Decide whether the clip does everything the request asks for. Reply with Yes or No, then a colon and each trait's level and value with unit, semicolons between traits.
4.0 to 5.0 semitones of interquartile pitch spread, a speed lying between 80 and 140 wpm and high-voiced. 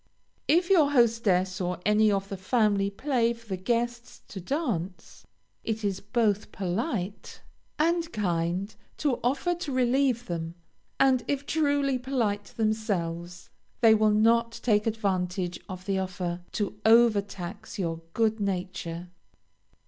Yes: average, 4.4 semitones; slow, 135 wpm; high, 215 Hz